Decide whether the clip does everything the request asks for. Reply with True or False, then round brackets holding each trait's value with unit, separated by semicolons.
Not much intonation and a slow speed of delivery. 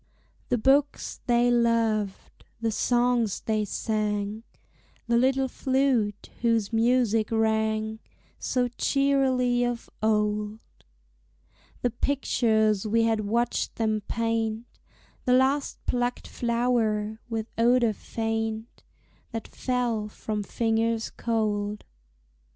True (2.1 semitones; 100 wpm)